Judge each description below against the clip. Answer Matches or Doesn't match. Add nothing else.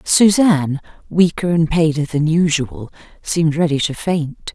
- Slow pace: Matches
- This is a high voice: Doesn't match